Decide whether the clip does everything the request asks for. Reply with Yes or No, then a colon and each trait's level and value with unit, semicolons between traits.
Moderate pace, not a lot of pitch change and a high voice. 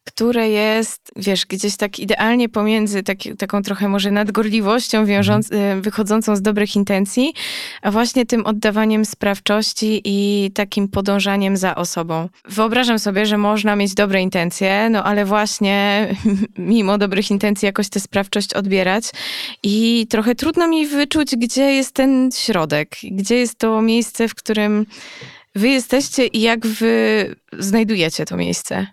Yes: average, 140 wpm; narrow, 2.2 semitones; high, 210 Hz